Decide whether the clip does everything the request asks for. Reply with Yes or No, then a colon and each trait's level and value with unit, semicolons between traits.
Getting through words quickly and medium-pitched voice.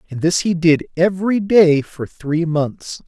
No: average, 175 wpm; medium, 165 Hz